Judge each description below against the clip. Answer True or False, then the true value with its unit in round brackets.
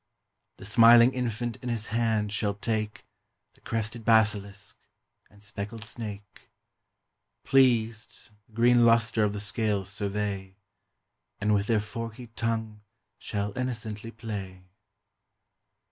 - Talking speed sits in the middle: False (115 wpm)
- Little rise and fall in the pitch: True (2.0 semitones)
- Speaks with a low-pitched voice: True (110 Hz)